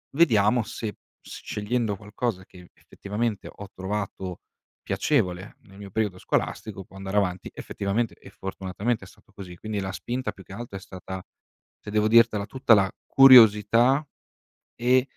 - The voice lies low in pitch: Yes, low, 105 Hz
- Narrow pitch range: No, average, 3.2 semitones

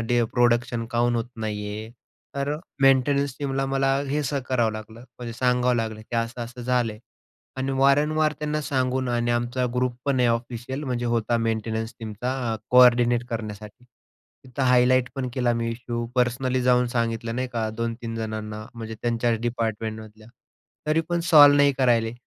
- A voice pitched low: Yes, low, 120 Hz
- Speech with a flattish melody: Yes, narrow, 2.1 semitones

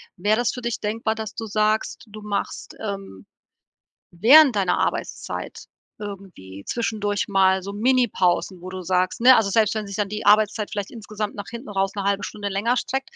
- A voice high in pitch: Yes, high, 210 Hz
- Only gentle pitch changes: Yes, narrow, 2.1 semitones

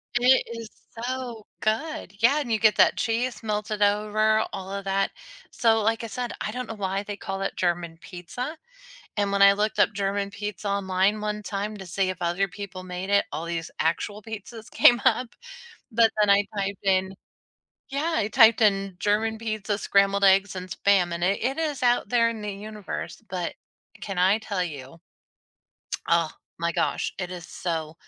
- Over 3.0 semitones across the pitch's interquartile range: No, average, 2.7 semitones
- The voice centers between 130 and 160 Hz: No, high, 205 Hz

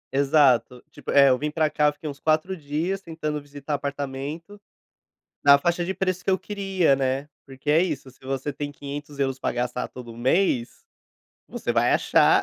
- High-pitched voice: No, medium, 145 Hz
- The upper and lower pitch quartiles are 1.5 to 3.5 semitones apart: Yes, average, 3.1 semitones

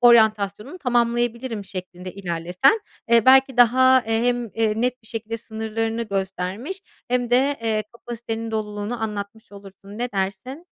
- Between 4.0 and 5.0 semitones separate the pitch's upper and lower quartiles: No, average, 3.0 semitones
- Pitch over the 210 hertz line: Yes, high, 225 Hz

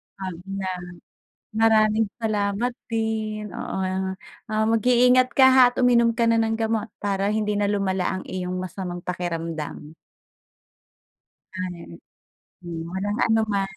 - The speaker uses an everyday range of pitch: Yes, average, 3.1 semitones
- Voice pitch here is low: No, high, 205 Hz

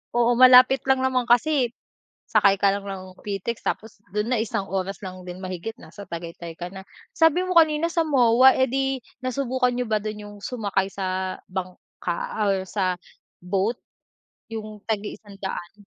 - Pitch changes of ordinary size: Yes, average, 5.0 semitones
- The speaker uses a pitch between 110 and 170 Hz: No, high, 210 Hz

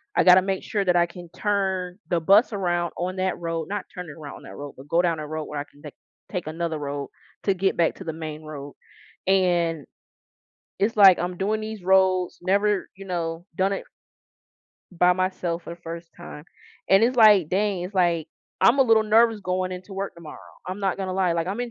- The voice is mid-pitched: Yes, medium, 180 Hz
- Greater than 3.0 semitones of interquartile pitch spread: No, average, 2.7 semitones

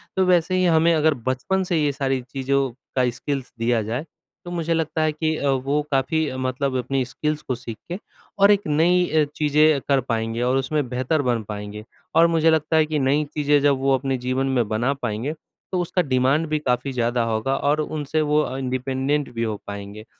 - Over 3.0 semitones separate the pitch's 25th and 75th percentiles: Yes, average, 3.6 semitones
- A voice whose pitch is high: No, medium, 140 Hz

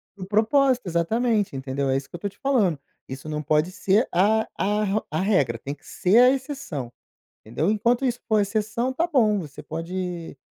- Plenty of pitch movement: Yes, wide, 6.6 semitones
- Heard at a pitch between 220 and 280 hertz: No, high, 200 Hz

